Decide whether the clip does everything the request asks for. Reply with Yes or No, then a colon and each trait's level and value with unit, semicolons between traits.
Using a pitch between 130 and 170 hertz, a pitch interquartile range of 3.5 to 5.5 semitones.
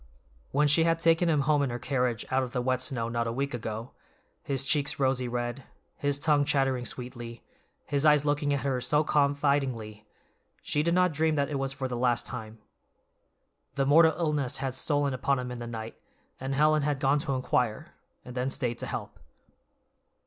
No: low, 135 Hz; average, 2.9 semitones